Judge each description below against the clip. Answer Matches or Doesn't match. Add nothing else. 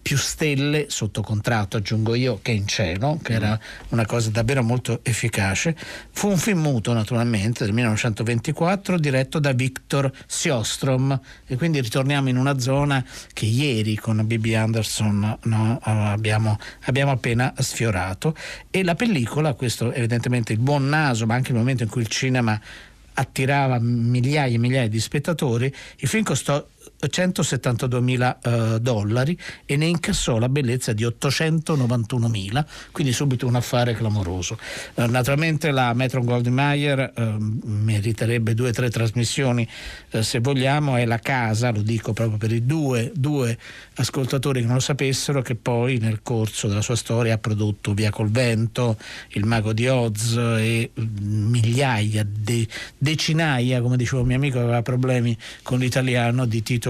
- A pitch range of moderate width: Matches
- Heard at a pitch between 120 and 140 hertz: Matches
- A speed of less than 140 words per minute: Doesn't match